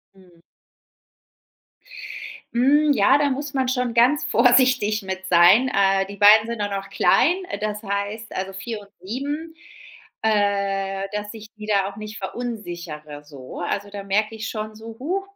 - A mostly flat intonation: No, average, 3.8 semitones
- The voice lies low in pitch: No, high, 210 Hz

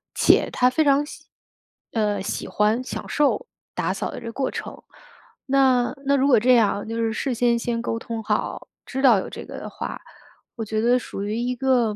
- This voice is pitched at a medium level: No, high, 240 Hz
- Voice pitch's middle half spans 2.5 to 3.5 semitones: Yes, average, 2.9 semitones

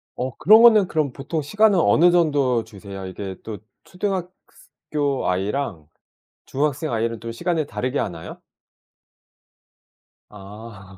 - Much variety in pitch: Yes, wide, 8.0 semitones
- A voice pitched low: Yes, low, 130 Hz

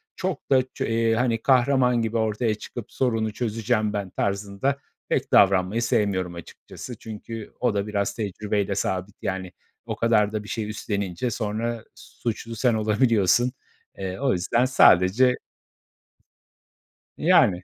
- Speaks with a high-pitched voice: No, low, 110 Hz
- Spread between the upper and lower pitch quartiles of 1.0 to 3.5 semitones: Yes, average, 2.9 semitones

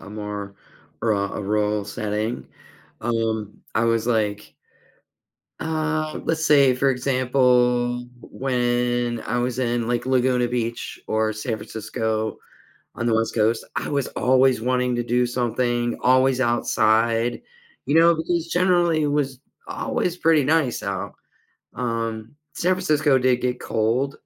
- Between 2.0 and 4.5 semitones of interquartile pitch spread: Yes, average, 2.9 semitones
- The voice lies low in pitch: Yes, low, 120 Hz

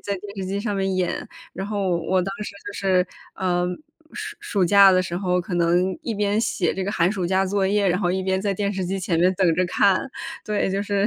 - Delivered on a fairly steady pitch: Yes, narrow, 1.8 semitones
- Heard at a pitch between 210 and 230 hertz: No, high, 190 Hz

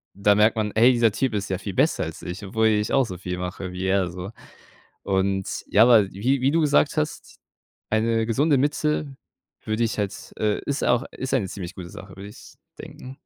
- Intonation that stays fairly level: No, average, 4.8 semitones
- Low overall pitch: Yes, low, 110 Hz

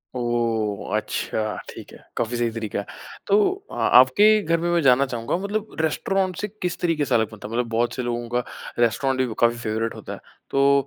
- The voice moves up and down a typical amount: No, wide, 5.7 semitones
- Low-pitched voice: Yes, low, 120 Hz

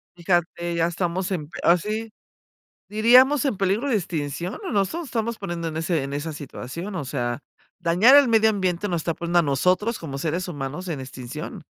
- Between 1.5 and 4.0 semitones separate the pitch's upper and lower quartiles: No, average, 4.9 semitones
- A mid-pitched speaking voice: Yes, medium, 175 Hz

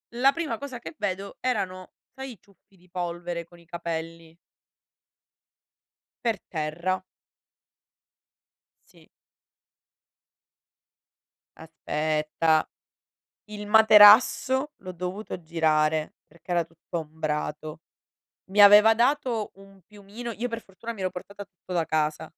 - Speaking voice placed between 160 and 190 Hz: Yes, medium, 185 Hz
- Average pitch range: Yes, average, 4.8 semitones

